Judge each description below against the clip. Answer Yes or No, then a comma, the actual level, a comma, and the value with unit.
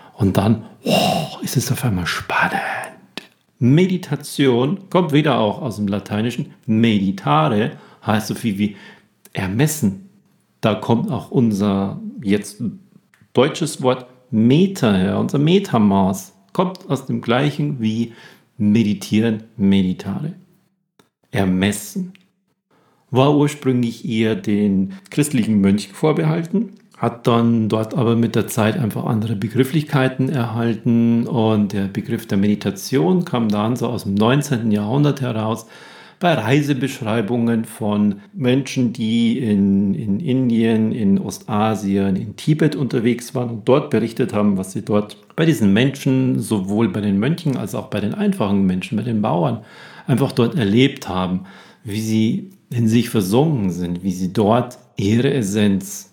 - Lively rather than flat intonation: Yes, wide, 5.8 semitones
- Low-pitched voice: Yes, low, 115 Hz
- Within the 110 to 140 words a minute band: Yes, average, 130 wpm